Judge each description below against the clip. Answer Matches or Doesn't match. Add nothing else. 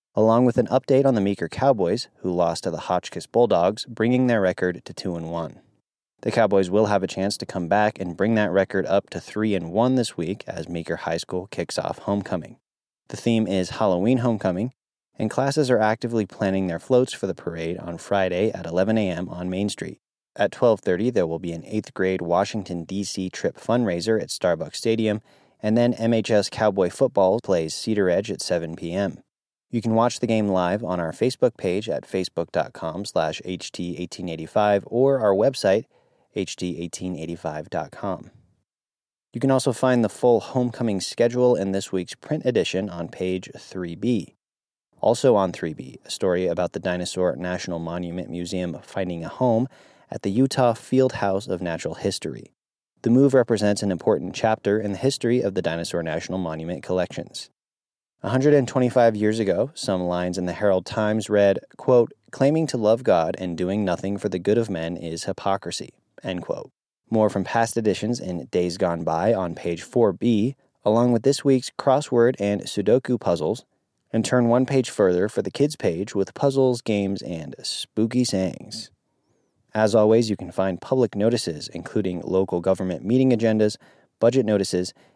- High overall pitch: Doesn't match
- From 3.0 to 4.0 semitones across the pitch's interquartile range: Doesn't match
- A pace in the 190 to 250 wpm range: Doesn't match